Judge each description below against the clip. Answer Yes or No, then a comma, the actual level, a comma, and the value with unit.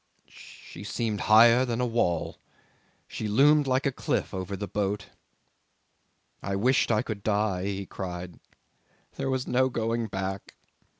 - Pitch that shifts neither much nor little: Yes, average, 3.9 semitones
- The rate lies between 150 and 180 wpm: No, average, 140 wpm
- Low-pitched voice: Yes, low, 110 Hz